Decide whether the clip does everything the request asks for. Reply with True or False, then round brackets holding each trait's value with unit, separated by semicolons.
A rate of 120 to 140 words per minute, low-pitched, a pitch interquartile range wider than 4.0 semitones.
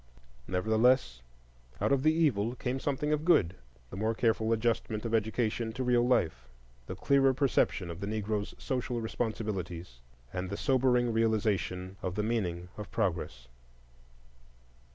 True (135 wpm; 110 Hz; 4.9 semitones)